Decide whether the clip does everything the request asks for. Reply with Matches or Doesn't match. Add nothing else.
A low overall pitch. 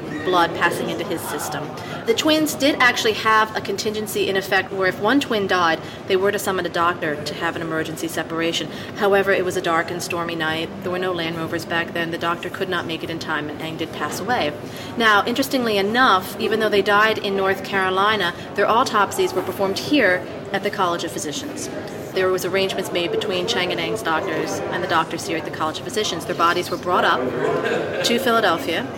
Doesn't match